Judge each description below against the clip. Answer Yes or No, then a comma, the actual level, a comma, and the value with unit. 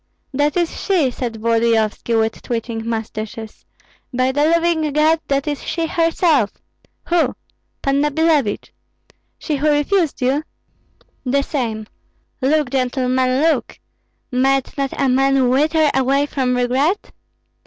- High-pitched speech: Yes, very high, 270 Hz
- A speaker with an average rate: No, slow, 120 wpm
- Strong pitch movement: No, average, 3.5 semitones